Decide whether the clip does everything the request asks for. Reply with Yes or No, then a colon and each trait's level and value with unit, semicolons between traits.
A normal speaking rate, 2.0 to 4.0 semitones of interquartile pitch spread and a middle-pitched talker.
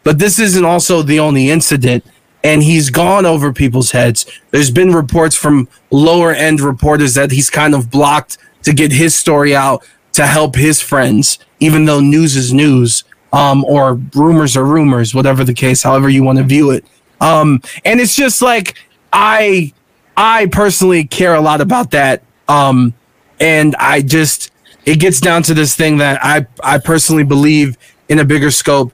Yes: average, 175 wpm; average, 2.9 semitones; medium, 150 Hz